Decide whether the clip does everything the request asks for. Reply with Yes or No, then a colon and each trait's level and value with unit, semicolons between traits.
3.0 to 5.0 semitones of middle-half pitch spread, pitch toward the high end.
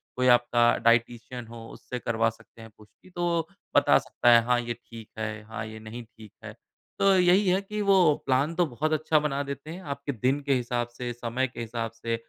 No: average, 4.4 semitones; low, 120 Hz